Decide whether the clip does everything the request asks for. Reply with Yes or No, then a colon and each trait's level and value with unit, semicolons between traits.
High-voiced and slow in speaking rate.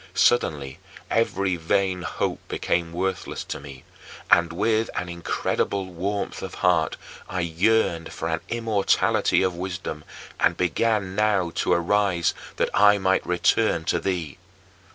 No: very low, 90 Hz; slow, 130 wpm